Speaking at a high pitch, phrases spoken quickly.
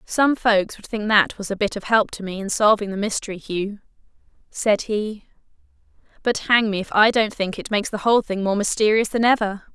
Yes: high, 210 Hz; fast, 215 wpm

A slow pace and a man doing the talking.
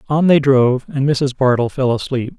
No: average, 200 wpm; male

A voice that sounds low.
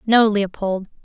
No: high, 205 Hz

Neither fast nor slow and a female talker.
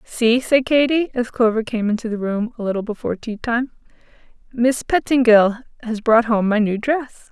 Yes: average, 180 wpm; female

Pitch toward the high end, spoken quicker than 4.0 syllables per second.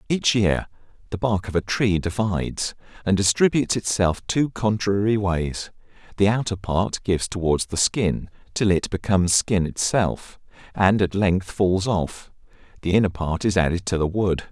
No: low, 100 Hz; 4.6 syllables/s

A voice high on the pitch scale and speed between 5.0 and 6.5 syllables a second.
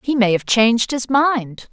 No: high, 240 Hz; 4.4 syllables/s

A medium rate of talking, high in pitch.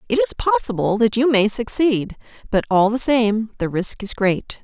Yes: average, 195 wpm; high, 215 Hz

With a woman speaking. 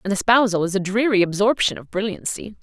Yes: female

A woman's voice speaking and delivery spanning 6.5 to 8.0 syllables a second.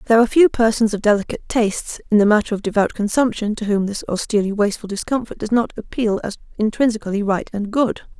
Yes: female; 6.7 syllables/s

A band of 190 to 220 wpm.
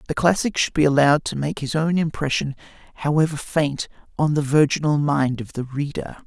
No: average, 180 wpm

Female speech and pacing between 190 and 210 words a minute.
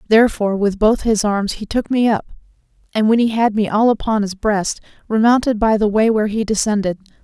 Yes: female; fast, 205 wpm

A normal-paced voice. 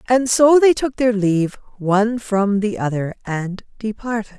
Yes: average, 165 wpm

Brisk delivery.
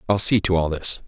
Yes: fast, 280 wpm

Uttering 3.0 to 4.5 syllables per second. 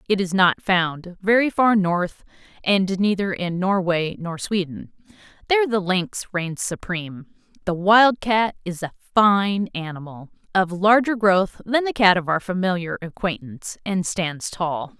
Yes: 4.2 syllables/s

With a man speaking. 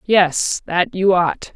No: female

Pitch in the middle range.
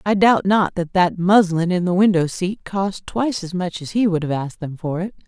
Yes: medium, 180 Hz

